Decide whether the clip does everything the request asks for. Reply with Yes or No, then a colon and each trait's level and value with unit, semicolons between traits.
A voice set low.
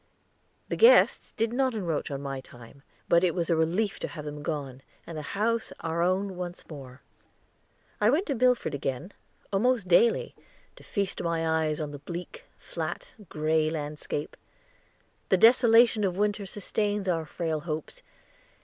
No: medium, 170 Hz